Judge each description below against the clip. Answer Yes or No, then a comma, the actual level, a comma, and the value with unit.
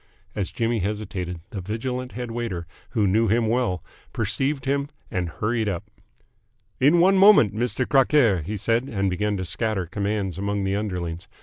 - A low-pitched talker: Yes, low, 105 Hz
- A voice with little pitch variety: No, average, 4.1 semitones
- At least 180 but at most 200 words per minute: No, average, 165 wpm